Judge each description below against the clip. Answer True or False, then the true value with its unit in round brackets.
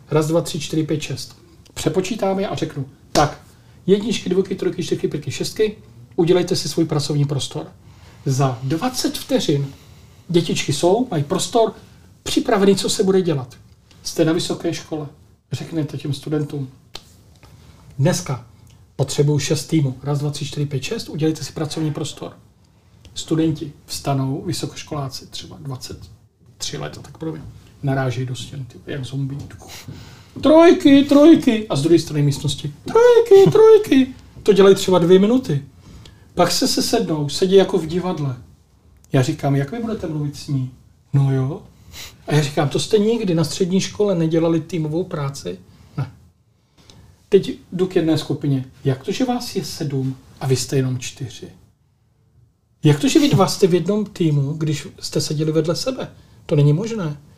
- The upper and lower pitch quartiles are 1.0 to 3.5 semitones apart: False (5.6 semitones)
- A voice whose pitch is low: False (150 Hz)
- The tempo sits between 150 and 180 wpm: True (155 wpm)